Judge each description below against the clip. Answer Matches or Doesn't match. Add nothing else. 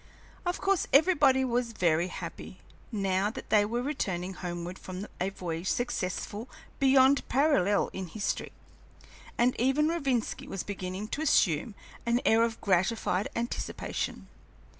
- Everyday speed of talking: Doesn't match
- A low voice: Doesn't match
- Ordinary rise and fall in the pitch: Doesn't match